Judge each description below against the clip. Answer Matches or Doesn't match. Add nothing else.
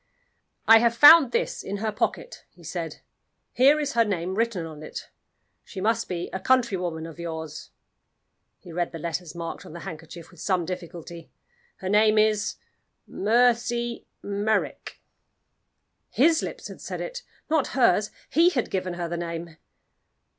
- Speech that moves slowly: Doesn't match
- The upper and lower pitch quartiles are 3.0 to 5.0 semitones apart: Doesn't match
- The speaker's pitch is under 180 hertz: Doesn't match